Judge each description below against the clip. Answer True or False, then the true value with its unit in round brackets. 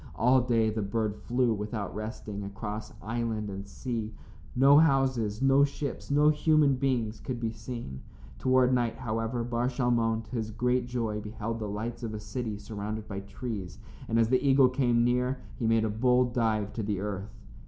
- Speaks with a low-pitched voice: True (115 Hz)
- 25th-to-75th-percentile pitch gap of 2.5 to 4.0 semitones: True (2.9 semitones)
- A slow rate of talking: False (180 wpm)